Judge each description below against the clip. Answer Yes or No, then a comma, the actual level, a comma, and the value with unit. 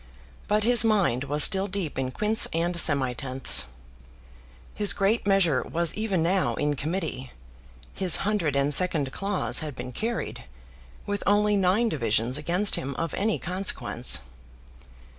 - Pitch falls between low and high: Yes, medium, 175 Hz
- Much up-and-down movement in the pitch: Yes, wide, 6.3 semitones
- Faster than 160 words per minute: No, average, 140 wpm